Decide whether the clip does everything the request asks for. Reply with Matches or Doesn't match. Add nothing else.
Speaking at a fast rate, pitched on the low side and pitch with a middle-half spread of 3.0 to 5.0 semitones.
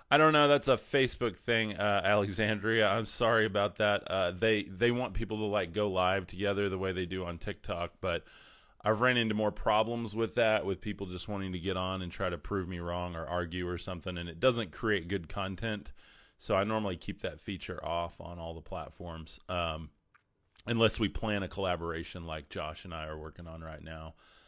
Matches